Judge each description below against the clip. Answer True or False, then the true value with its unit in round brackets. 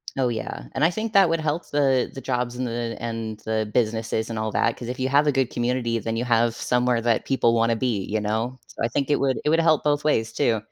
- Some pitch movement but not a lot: True (3.1 semitones)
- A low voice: True (120 Hz)